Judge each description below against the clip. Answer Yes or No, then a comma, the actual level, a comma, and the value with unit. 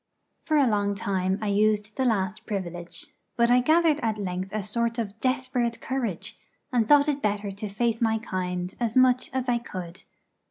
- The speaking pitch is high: Yes, high, 220 Hz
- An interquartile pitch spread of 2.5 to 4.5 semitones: Yes, average, 3.8 semitones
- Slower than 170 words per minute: No, average, 185 wpm